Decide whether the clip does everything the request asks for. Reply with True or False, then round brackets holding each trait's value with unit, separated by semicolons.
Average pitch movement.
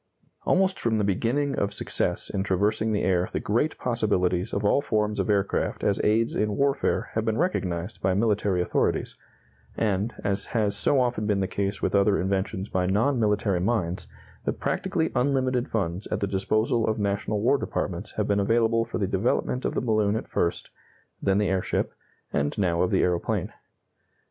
True (3.0 semitones)